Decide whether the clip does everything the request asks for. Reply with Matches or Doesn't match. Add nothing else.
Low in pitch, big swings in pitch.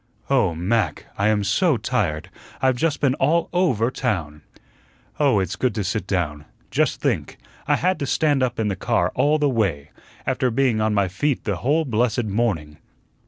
Matches